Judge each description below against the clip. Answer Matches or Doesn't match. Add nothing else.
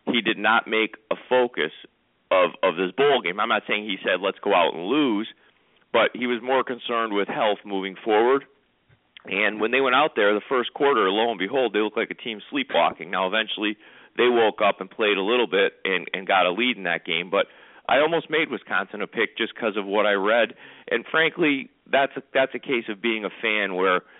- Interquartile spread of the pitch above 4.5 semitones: Doesn't match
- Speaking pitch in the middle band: Doesn't match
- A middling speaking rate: Doesn't match